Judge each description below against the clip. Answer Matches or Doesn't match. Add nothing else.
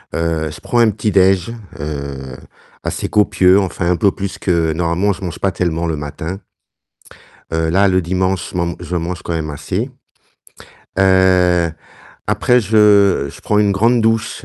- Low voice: Matches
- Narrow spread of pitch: Doesn't match